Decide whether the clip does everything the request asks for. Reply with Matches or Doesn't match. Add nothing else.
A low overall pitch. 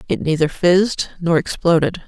Doesn't match